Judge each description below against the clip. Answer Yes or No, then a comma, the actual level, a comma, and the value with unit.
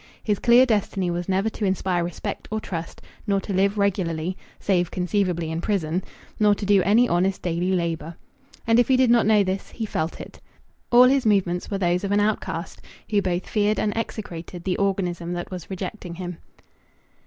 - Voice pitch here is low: No, high, 190 Hz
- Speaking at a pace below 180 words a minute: No, average, 190 wpm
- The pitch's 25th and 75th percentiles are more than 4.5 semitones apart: No, average, 2.9 semitones